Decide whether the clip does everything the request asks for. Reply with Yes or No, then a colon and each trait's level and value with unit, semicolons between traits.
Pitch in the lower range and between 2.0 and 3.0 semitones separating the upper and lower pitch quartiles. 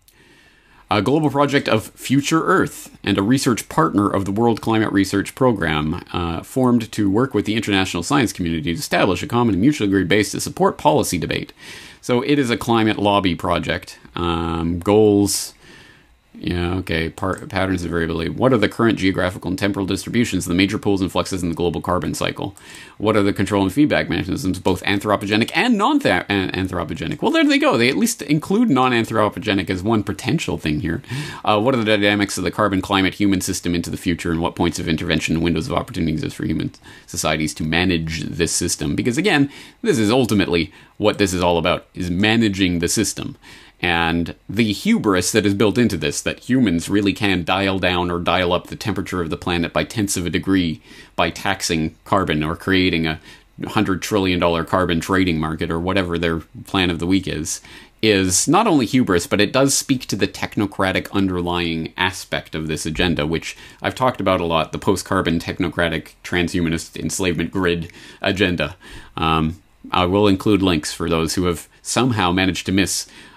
No: very low, 95 Hz; average, 3.6 semitones